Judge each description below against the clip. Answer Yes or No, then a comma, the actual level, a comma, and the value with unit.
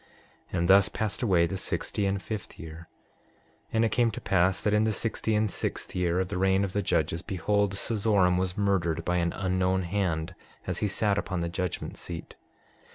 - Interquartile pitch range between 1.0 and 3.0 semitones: Yes, narrow, 2.6 semitones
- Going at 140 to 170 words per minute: No, average, 200 wpm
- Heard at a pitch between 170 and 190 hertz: No, very low, 95 Hz